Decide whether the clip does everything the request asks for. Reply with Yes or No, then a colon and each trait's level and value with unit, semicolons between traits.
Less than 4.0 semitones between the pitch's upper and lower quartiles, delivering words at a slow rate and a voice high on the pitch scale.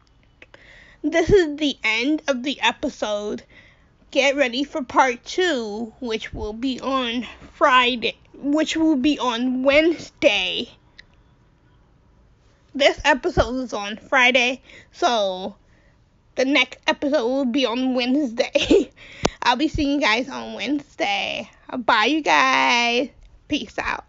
Yes: average, 3.4 semitones; slow, 120 wpm; very high, 275 Hz